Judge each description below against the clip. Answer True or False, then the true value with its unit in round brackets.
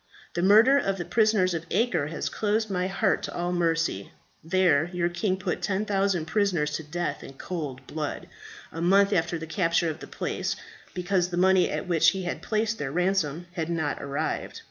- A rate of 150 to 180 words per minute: False (190 wpm)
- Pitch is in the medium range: True (175 Hz)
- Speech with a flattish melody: False (3.1 semitones)